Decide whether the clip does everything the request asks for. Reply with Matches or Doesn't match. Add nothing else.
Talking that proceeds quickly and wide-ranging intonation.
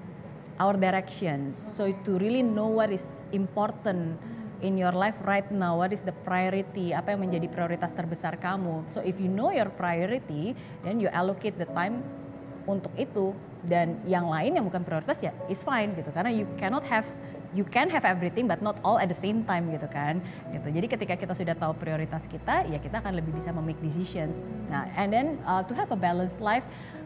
Doesn't match